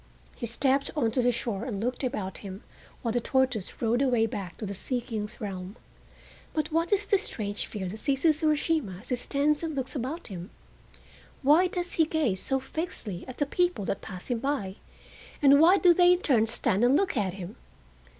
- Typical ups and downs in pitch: No, wide, 6.4 semitones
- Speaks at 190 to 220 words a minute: Yes, average, 200 wpm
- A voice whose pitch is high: Yes, very high, 250 Hz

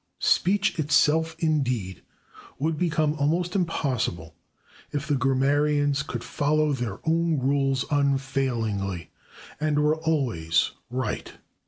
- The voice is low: No, medium, 145 Hz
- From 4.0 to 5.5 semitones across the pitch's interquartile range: No, average, 3.3 semitones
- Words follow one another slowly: Yes, slow, 105 wpm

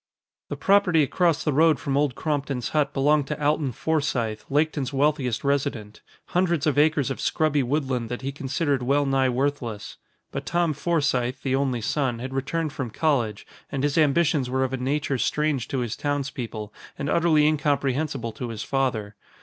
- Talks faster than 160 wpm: Yes, average, 170 wpm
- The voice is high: No, medium, 140 Hz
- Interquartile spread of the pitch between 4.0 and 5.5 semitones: No, average, 2.9 semitones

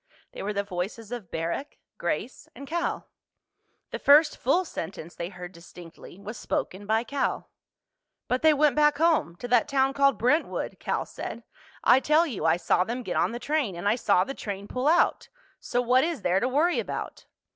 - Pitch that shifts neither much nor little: No, wide, 6.9 semitones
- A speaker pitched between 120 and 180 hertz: No, high, 245 Hz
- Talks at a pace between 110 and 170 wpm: No, average, 190 wpm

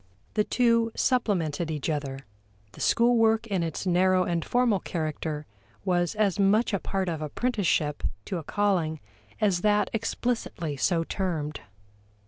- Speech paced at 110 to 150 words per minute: Yes, average, 140 wpm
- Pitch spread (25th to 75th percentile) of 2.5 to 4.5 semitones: No, average, 5.1 semitones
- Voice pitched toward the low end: No, medium, 185 Hz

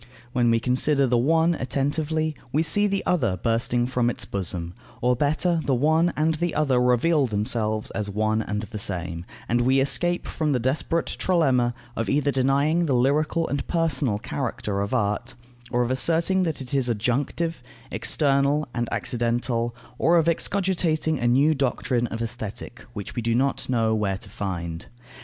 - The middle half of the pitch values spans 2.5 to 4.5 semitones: No, average, 5.1 semitones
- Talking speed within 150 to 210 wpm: Yes, average, 170 wpm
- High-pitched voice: No, low, 130 Hz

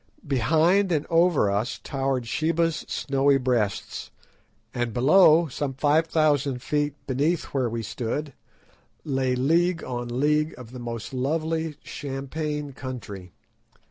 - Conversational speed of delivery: No, slow, 120 wpm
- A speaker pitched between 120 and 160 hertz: Yes, medium, 140 Hz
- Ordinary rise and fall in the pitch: Yes, average, 3.8 semitones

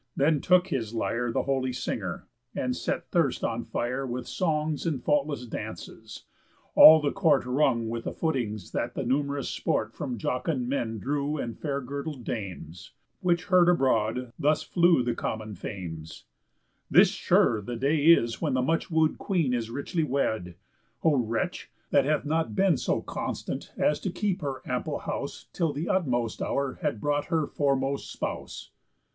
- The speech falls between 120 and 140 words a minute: No, average, 165 wpm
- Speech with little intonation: No, average, 4.6 semitones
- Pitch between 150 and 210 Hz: No, medium, 140 Hz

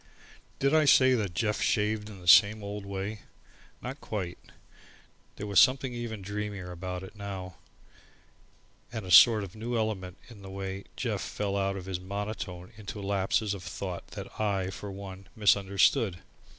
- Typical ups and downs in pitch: No, narrow, 2.2 semitones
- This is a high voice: No, low, 100 Hz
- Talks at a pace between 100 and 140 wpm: No, average, 165 wpm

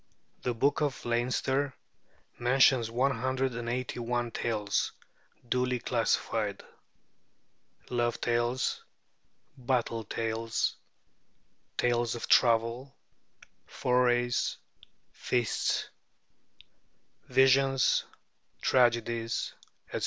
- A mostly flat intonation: Yes, narrow, 1.6 semitones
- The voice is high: No, low, 120 Hz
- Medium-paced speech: No, slow, 75 wpm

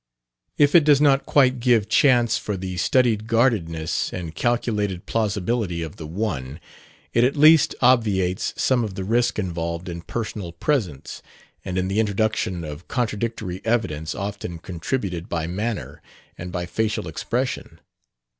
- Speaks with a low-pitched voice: Yes, low, 105 Hz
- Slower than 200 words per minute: Yes, average, 145 wpm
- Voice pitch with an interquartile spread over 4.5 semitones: Yes, average, 5.3 semitones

